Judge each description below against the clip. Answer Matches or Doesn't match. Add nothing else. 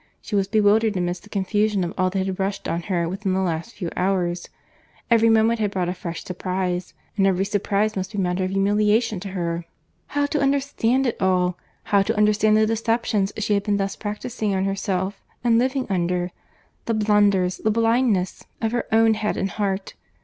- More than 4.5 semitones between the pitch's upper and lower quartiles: Doesn't match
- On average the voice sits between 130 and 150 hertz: Doesn't match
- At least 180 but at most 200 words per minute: Matches